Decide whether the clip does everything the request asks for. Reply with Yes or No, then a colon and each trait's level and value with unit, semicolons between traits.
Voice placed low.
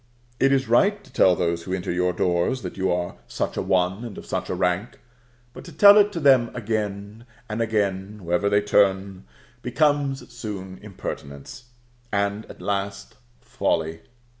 Yes: low, 100 Hz